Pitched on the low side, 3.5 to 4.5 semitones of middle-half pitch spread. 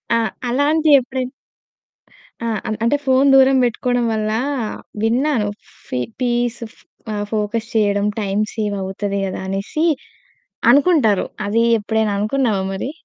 No: high, 225 Hz; average, 4.1 semitones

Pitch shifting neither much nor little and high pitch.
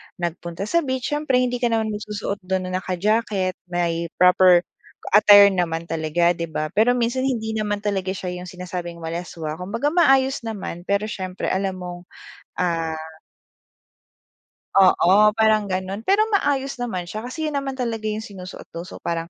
Yes: average, 4.3 semitones; high, 195 Hz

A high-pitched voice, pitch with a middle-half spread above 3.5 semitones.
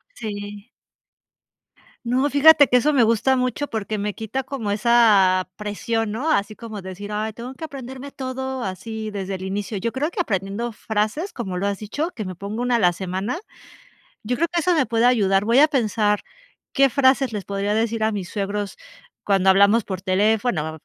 Yes: high, 220 Hz; average, 4.1 semitones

